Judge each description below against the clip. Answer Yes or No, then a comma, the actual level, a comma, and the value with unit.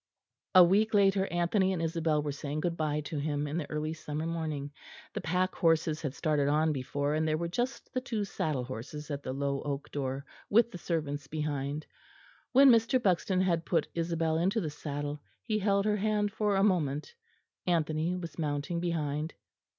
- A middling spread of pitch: Yes, average, 4.0 semitones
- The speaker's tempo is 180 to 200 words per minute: Yes, average, 185 wpm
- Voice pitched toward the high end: No, medium, 160 Hz